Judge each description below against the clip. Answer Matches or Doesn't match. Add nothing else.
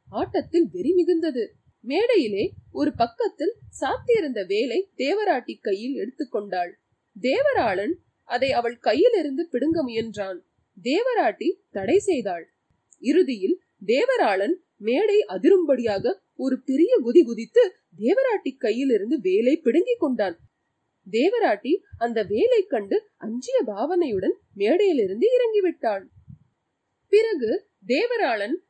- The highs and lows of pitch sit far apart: Matches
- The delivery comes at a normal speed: Doesn't match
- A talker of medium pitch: Doesn't match